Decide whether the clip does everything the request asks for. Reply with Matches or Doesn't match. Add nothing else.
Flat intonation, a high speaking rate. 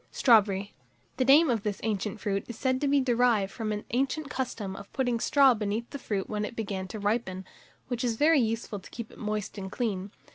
Doesn't match